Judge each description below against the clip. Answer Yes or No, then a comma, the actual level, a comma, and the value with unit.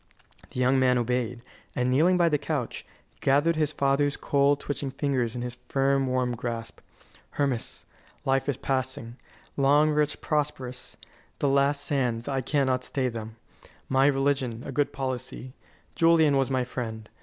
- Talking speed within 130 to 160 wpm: Yes, average, 150 wpm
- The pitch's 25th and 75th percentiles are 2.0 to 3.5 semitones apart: Yes, narrow, 2.4 semitones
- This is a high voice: No, low, 135 Hz